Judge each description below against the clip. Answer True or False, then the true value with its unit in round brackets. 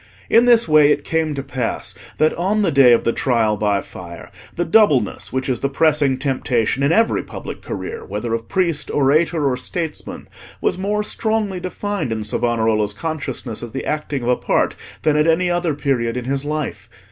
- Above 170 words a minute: True (190 wpm)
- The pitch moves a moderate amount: False (5.7 semitones)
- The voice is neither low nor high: True (145 Hz)